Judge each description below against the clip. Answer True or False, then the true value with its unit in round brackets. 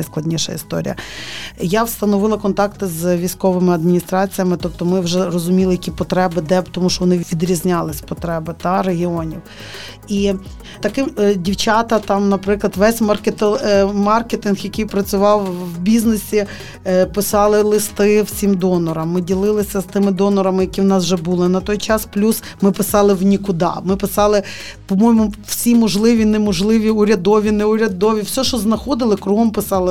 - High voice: True (200 Hz)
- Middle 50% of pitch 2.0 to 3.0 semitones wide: True (2.4 semitones)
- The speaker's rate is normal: True (135 wpm)